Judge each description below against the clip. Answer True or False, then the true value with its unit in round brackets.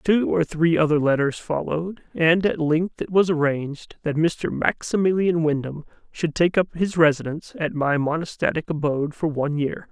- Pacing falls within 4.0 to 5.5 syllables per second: True (4.9 syllables/s)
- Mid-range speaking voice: True (160 Hz)